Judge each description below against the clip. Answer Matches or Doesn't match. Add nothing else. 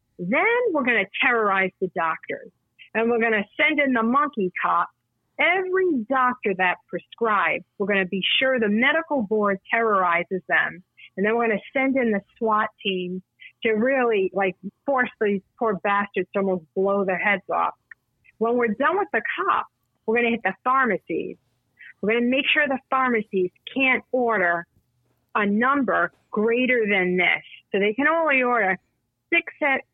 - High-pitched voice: Matches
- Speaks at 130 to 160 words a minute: Doesn't match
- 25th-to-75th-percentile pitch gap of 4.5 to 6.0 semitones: Matches